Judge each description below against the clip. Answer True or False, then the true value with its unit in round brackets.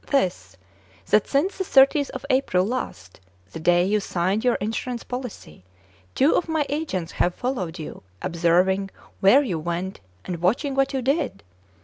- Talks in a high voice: True (210 Hz)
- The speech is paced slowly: False (155 wpm)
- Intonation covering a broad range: True (7.5 semitones)